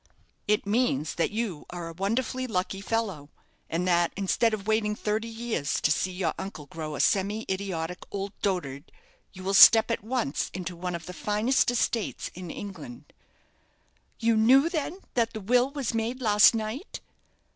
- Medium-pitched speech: No, high, 205 Hz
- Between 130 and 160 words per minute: No, average, 170 wpm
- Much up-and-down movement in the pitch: No, average, 4.2 semitones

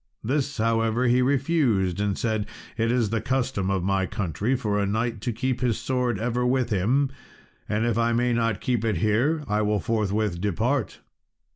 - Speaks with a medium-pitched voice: No, low, 115 Hz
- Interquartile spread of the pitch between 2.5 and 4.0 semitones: Yes, average, 3.2 semitones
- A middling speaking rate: Yes, average, 180 wpm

